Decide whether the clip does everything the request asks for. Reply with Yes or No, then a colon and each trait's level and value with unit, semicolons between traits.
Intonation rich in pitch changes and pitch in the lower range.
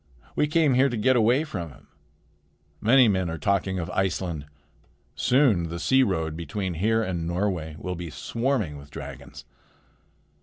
Yes: wide, 6.4 semitones; very low, 95 Hz